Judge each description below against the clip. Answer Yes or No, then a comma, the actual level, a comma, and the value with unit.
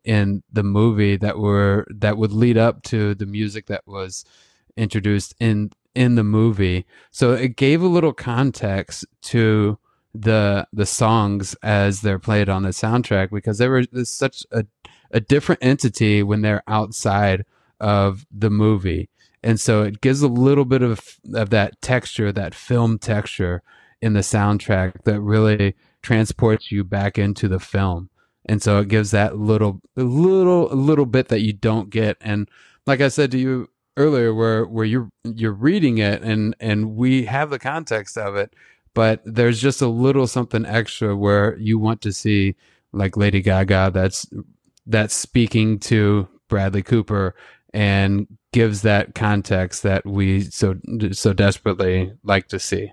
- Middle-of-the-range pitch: No, low, 110 Hz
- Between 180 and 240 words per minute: No, average, 160 wpm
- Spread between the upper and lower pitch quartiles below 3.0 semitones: Yes, narrow, 2.6 semitones